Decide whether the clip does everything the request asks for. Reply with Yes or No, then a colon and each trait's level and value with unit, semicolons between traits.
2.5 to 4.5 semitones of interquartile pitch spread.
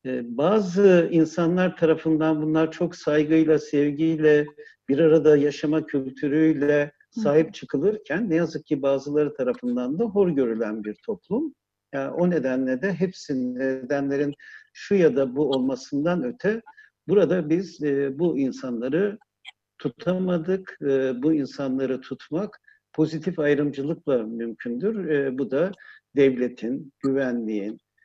No: wide, 5.5 semitones